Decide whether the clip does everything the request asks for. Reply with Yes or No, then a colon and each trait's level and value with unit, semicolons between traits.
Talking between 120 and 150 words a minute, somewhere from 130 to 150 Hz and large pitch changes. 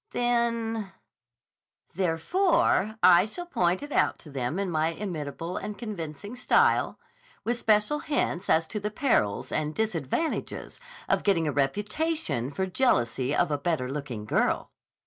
No: average, 140 wpm; medium, 185 Hz; wide, 7.2 semitones